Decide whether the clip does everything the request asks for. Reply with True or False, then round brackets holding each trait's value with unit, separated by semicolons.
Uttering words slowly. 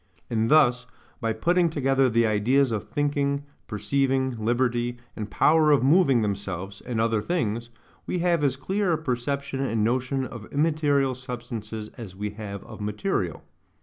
False (150 wpm)